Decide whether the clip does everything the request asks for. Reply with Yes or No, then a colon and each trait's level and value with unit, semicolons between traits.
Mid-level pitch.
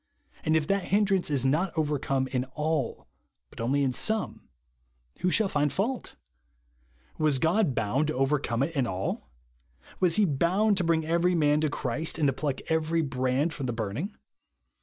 Yes: medium, 150 Hz